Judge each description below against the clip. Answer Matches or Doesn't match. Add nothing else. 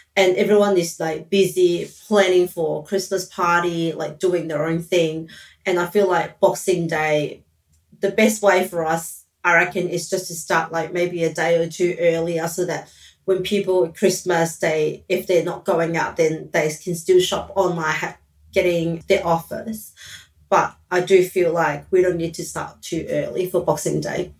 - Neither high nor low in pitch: Matches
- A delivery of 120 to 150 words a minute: Doesn't match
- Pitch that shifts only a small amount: Matches